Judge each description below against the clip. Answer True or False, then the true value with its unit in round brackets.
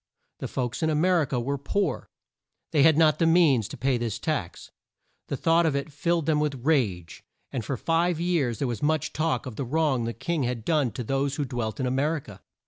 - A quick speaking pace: True (235 wpm)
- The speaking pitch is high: False (140 Hz)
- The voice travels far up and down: False (4.5 semitones)